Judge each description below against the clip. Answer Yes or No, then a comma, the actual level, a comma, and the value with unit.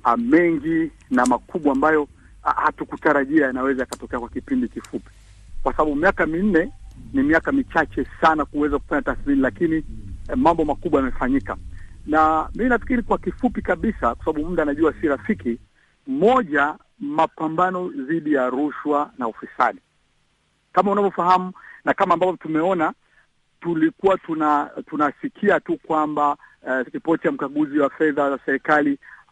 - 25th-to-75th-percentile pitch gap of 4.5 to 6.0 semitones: Yes, wide, 5.6 semitones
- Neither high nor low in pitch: Yes, medium, 155 Hz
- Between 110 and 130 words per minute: Yes, average, 120 wpm